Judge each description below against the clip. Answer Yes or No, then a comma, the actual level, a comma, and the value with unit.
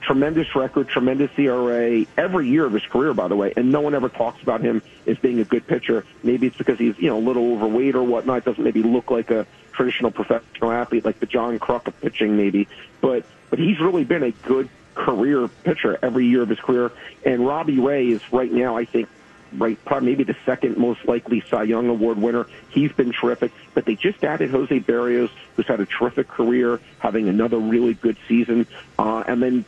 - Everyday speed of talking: No, fast, 210 wpm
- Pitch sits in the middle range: No, low, 120 Hz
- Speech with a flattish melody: Yes, narrow, 1.7 semitones